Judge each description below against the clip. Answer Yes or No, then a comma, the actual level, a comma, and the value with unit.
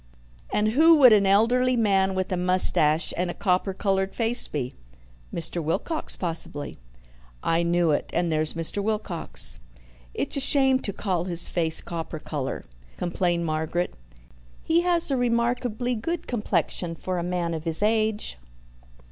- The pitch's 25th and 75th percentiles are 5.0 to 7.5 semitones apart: Yes, average, 5.3 semitones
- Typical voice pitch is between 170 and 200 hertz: Yes, medium, 185 Hz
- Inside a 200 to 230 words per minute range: No, average, 150 wpm